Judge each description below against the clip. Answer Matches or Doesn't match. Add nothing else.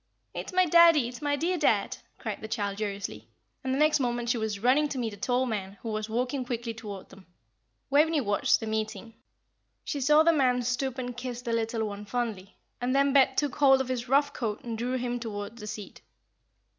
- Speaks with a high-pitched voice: Matches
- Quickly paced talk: Matches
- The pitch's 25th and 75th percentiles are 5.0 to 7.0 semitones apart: Doesn't match